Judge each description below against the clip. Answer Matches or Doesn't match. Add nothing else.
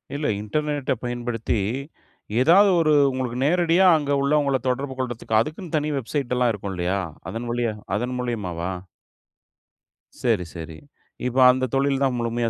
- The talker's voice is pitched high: Doesn't match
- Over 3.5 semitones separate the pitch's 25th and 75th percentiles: Matches